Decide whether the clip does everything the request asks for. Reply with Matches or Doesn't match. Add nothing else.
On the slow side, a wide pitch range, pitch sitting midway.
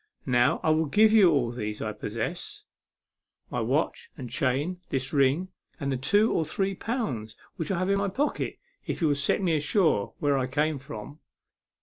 Doesn't match